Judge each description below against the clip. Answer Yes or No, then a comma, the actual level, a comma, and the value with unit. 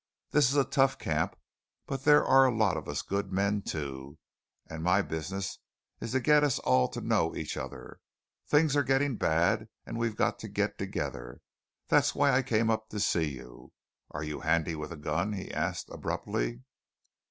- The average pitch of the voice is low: Yes, low, 100 Hz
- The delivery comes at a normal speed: Yes, average, 185 wpm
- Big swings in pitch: Yes, wide, 8.8 semitones